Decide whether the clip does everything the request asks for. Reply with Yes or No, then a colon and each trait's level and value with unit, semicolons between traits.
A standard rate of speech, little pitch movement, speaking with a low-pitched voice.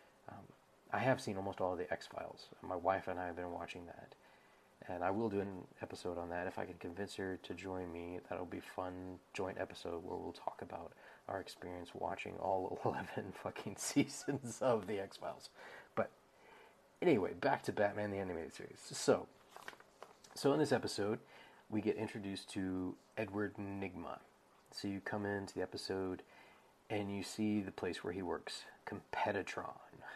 Yes: average, 175 wpm; narrow, 2.1 semitones; very low, 95 Hz